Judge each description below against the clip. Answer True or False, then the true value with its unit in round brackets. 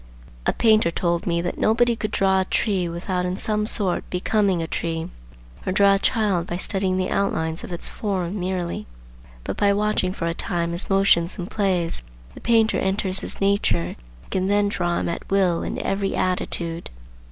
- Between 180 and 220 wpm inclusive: True (185 wpm)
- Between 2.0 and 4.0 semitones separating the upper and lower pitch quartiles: True (2.8 semitones)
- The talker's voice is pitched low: False (185 Hz)